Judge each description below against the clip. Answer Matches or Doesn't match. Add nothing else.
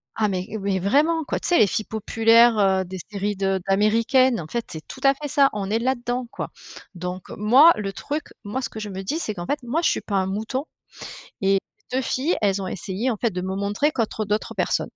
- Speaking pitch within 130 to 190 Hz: Doesn't match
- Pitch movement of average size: Matches